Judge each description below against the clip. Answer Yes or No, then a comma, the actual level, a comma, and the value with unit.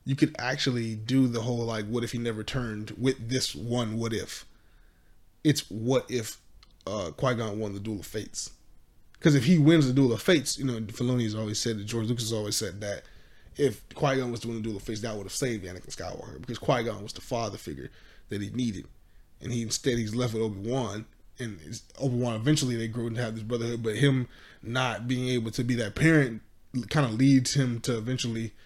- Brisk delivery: Yes, fast, 225 wpm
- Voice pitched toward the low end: Yes, low, 115 Hz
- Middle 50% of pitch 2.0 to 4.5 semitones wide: Yes, average, 2.8 semitones